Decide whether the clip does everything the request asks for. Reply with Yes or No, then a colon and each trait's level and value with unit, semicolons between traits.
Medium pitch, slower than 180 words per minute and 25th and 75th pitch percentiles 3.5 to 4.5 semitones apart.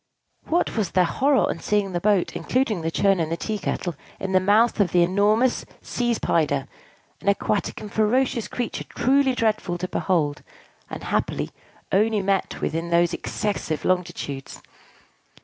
No: high, 195 Hz; average, 160 wpm; average, 4.2 semitones